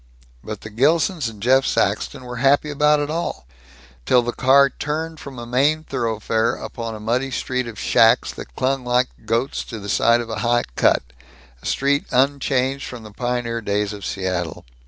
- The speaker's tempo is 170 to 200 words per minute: Yes, average, 180 wpm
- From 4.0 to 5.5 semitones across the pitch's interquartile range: No, average, 3.4 semitones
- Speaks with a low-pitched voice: Yes, low, 125 Hz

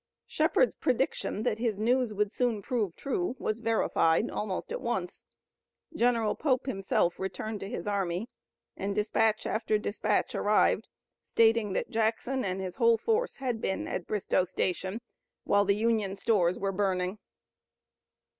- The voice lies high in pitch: Yes, high, 215 Hz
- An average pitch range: Yes, average, 3.0 semitones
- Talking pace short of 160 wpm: Yes, average, 145 wpm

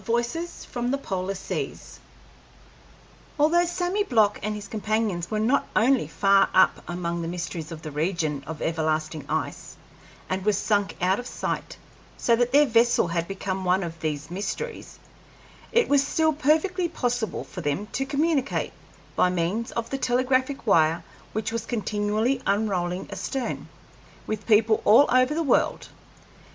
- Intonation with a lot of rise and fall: Yes, wide, 6.3 semitones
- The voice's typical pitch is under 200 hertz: No, high, 215 Hz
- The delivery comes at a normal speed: Yes, average, 150 wpm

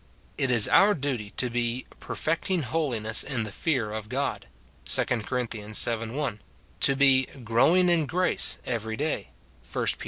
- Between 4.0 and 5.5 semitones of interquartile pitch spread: Yes, average, 5.0 semitones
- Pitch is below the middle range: Yes, low, 125 Hz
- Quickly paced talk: No, average, 155 wpm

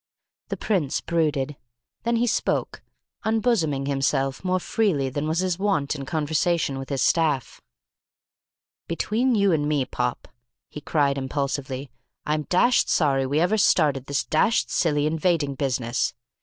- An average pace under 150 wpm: Yes, average, 140 wpm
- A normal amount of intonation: Yes, average, 4.6 semitones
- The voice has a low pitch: No, medium, 150 Hz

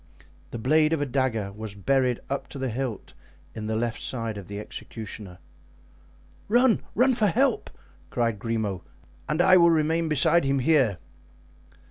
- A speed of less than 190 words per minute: Yes, average, 155 wpm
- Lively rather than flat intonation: Yes, wide, 6.2 semitones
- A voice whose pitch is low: Yes, low, 130 Hz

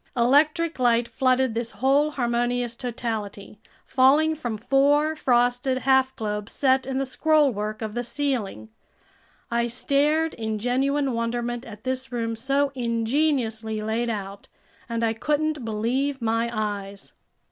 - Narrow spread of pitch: No, average, 3.3 semitones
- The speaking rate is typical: No, slow, 130 wpm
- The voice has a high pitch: Yes, high, 245 Hz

